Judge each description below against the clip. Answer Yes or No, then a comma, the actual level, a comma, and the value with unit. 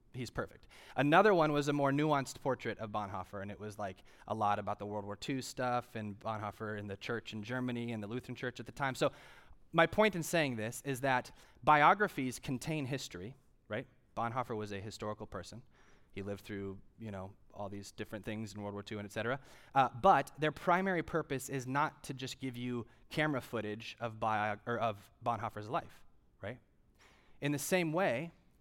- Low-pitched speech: Yes, low, 120 Hz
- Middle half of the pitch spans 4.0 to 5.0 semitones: Yes, average, 4.5 semitones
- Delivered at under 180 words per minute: No, average, 195 wpm